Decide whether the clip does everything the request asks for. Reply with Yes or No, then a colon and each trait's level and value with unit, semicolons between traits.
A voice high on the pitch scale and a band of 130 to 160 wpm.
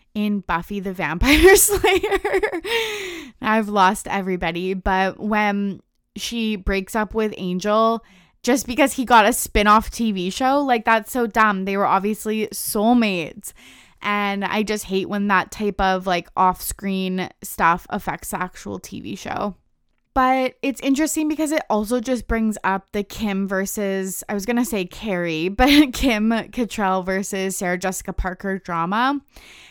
Yes: high, 210 Hz; average, 150 wpm